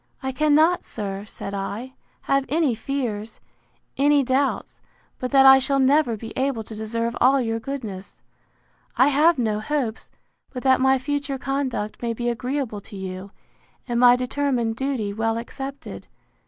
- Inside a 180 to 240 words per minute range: No, average, 155 wpm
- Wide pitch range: No, average, 3.7 semitones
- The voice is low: No, very high, 255 Hz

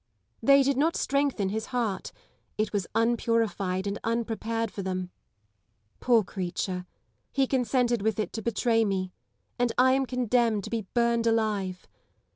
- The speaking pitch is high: Yes, high, 225 Hz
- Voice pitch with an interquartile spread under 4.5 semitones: Yes, average, 3.4 semitones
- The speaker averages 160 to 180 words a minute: No, average, 145 wpm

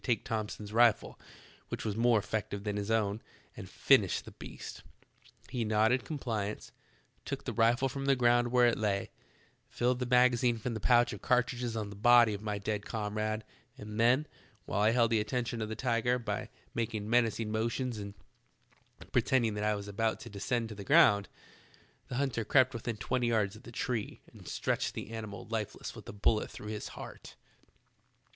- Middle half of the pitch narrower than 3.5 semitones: Yes, narrow, 2.4 semitones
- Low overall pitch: Yes, low, 115 Hz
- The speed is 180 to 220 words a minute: Yes, average, 185 wpm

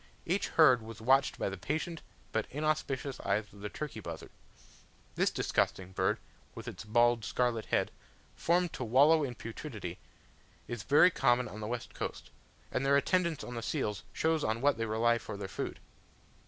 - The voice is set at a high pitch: No, low, 120 Hz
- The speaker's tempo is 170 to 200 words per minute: Yes, average, 175 wpm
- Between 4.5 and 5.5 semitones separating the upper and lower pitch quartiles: Yes, average, 5.2 semitones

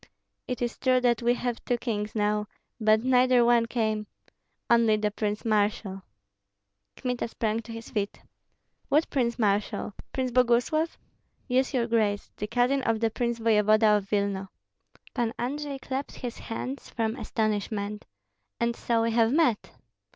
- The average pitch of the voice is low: No, high, 230 Hz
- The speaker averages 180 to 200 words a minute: No, average, 150 wpm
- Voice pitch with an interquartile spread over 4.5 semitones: No, narrow, 2.6 semitones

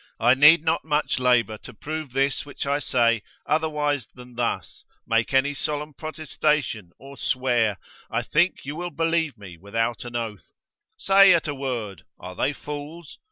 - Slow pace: No, average, 160 wpm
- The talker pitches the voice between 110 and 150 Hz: Yes, medium, 140 Hz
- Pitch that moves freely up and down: No, average, 4.6 semitones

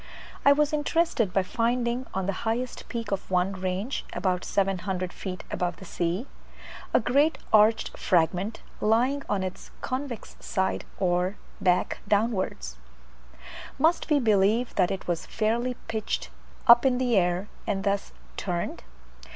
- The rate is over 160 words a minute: No, average, 140 wpm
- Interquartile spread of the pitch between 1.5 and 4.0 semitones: No, average, 4.6 semitones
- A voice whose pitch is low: No, high, 205 Hz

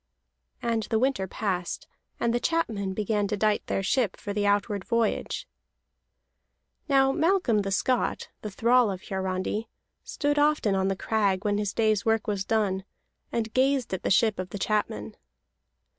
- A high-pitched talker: Yes, high, 210 Hz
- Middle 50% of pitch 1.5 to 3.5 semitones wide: Yes, average, 3.2 semitones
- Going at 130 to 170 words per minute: Yes, average, 160 wpm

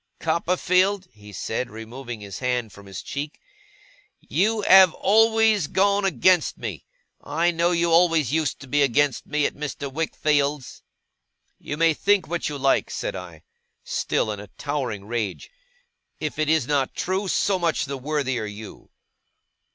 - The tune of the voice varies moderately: No, wide, 5.9 semitones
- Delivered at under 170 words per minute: Yes, average, 150 wpm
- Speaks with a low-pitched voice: No, medium, 150 Hz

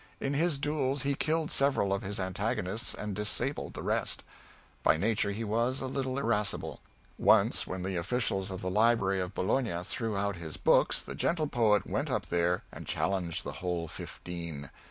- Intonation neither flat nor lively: No, wide, 5.9 semitones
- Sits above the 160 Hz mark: No, low, 105 Hz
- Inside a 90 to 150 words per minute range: No, average, 175 wpm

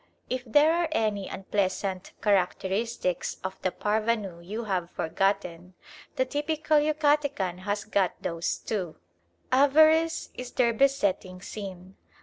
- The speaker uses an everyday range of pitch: No, wide, 6.5 semitones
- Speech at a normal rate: No, slow, 120 wpm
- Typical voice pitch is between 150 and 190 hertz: No, high, 210 Hz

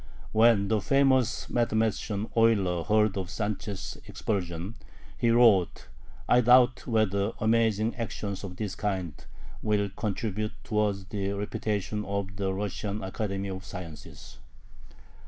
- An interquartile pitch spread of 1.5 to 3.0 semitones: Yes, narrow, 2.4 semitones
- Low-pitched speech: Yes, low, 105 Hz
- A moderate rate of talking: No, slow, 120 wpm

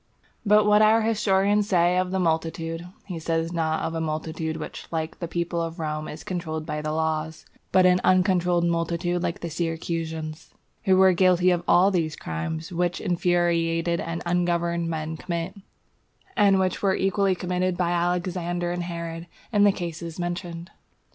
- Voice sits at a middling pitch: Yes, medium, 170 Hz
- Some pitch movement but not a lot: No, narrow, 1.8 semitones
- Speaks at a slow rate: No, average, 165 wpm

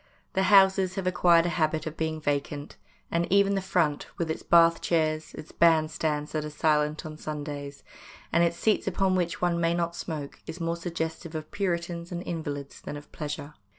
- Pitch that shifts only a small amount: Yes, narrow, 2.3 semitones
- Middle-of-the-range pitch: Yes, medium, 165 Hz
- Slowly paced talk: No, average, 190 wpm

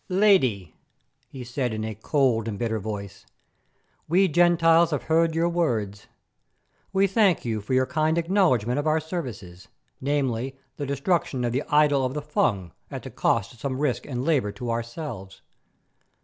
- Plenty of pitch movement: Yes, wide, 6.2 semitones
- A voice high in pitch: No, low, 135 Hz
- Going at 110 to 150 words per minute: No, average, 165 wpm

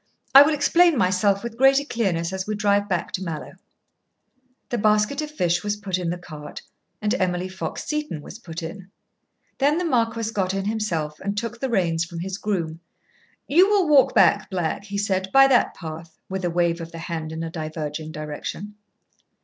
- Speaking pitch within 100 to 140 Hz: No, high, 190 Hz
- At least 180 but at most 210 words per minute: Yes, average, 190 wpm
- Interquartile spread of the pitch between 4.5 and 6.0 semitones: Yes, wide, 5.4 semitones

